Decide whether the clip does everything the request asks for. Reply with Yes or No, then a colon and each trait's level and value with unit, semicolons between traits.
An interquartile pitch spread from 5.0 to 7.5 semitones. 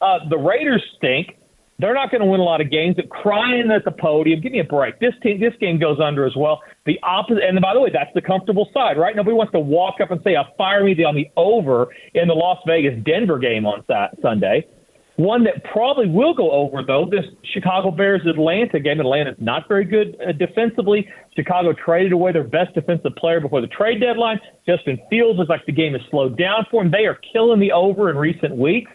Yes: wide, 5.4 semitones